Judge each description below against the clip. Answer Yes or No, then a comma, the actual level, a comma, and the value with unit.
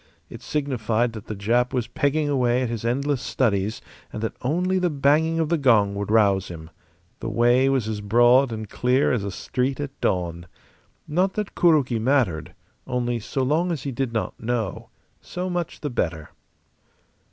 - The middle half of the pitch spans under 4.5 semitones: No, average, 4.8 semitones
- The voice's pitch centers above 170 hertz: No, low, 125 Hz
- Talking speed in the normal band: Yes, average, 175 wpm